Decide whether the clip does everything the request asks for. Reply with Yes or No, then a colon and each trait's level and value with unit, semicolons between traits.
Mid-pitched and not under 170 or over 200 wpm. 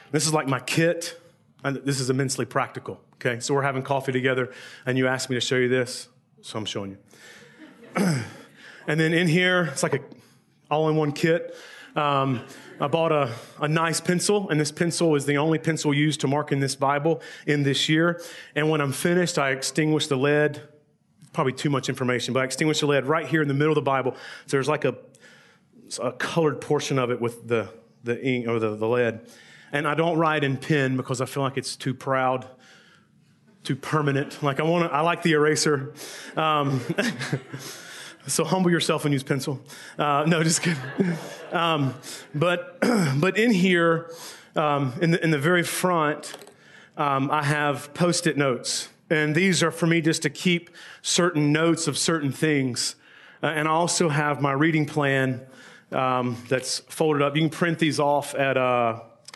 Yes: medium, 150 Hz; average, 190 wpm